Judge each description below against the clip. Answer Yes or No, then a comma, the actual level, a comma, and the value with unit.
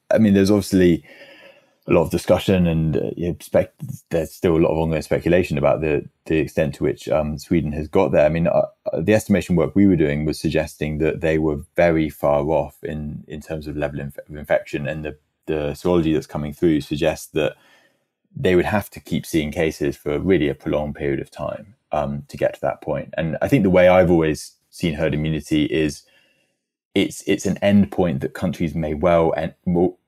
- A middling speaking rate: No, fast, 215 wpm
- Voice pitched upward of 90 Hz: No, very low, 80 Hz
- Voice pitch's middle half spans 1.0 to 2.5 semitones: No, average, 2.9 semitones